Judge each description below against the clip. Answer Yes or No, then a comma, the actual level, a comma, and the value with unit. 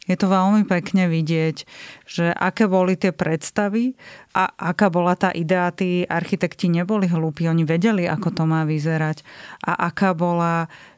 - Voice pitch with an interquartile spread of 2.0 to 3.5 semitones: Yes, narrow, 2.4 semitones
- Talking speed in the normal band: Yes, average, 155 wpm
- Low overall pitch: No, medium, 175 Hz